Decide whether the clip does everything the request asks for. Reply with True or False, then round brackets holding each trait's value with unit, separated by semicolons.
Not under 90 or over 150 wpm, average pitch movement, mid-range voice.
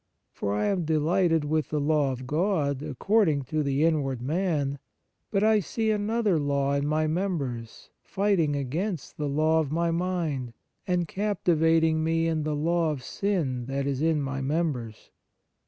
False (160 wpm; 3.7 semitones; 155 Hz)